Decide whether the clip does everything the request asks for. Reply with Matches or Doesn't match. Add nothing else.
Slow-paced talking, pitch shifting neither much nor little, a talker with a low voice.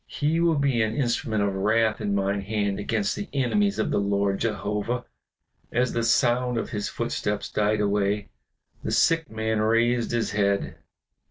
Doesn't match